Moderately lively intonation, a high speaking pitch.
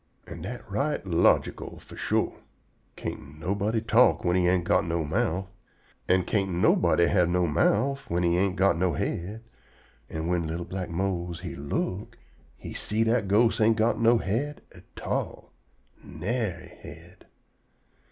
No: average, 4.2 semitones; very low, 95 Hz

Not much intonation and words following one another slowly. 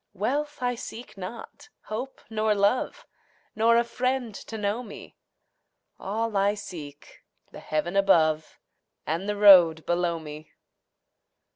No: average, 5.1 semitones; slow, 125 wpm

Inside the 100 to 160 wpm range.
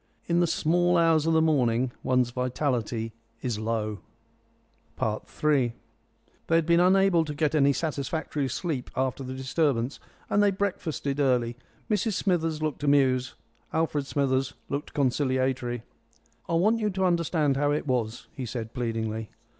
Yes: average, 145 wpm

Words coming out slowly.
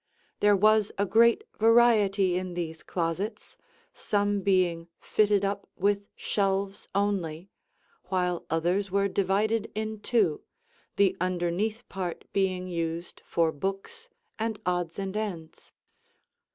Yes: slow, 115 wpm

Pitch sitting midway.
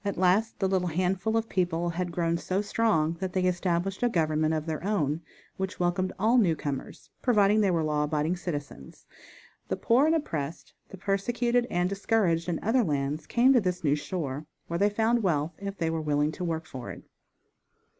Yes: medium, 180 Hz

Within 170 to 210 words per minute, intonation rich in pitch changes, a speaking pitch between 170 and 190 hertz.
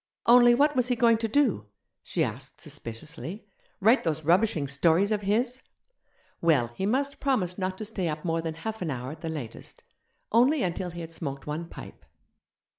Yes: average, 185 wpm; wide, 6.4 semitones; medium, 185 Hz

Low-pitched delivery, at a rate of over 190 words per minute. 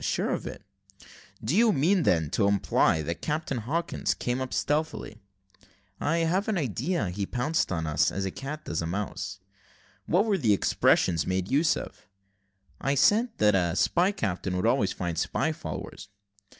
No: low, 115 Hz; average, 170 wpm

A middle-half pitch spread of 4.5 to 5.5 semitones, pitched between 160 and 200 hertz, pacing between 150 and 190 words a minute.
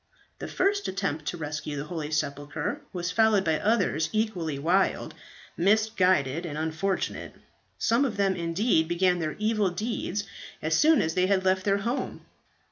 Yes: average, 4.9 semitones; medium, 185 Hz; average, 155 wpm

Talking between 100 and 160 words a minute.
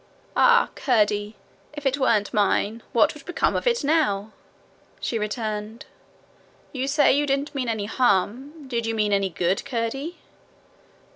Yes: average, 145 wpm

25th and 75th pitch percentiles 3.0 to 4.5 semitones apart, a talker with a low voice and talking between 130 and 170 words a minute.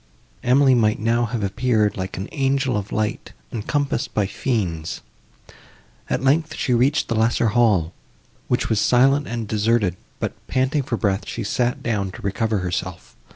Yes: average, 3.9 semitones; low, 115 Hz; average, 155 wpm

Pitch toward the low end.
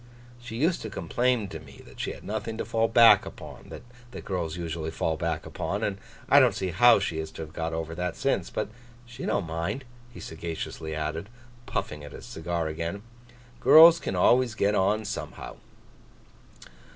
Yes: very low, 95 Hz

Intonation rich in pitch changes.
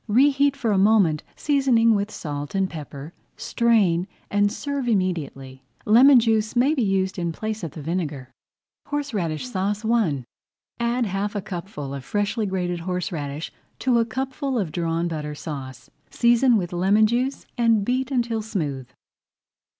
Yes: wide, 6.0 semitones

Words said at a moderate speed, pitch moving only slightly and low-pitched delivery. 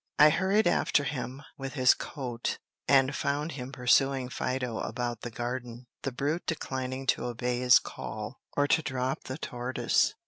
Yes: average, 160 wpm; narrow, 2.2 semitones; low, 130 Hz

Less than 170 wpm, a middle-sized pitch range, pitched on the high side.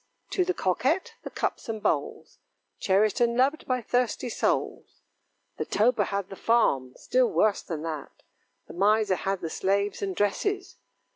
Yes: average, 155 wpm; average, 4.7 semitones; high, 215 Hz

